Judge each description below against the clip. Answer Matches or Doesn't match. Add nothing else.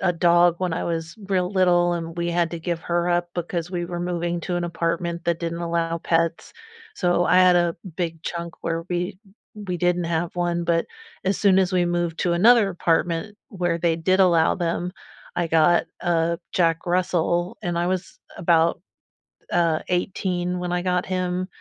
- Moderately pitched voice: Matches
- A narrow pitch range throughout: Matches